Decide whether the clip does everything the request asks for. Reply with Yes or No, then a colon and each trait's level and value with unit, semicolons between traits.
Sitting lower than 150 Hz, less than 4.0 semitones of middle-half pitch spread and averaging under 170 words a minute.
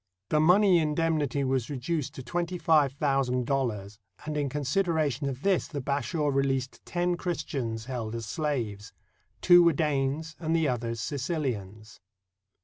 No: medium, 140 Hz; average, 4.3 semitones; average, 145 wpm